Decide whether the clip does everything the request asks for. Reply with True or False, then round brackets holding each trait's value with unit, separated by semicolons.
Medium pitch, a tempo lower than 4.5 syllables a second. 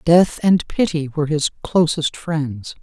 True (160 Hz; 4.0 syllables/s)